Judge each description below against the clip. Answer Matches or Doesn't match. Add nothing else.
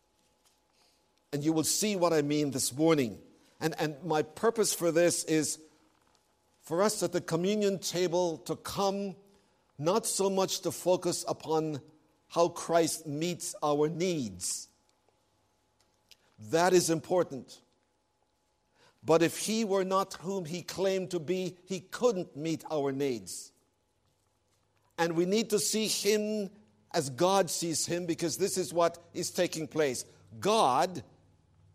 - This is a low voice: Doesn't match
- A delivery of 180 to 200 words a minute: Doesn't match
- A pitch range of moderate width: Matches